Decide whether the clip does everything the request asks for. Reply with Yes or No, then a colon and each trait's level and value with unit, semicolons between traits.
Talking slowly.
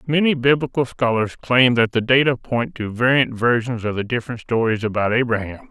No: average, 180 wpm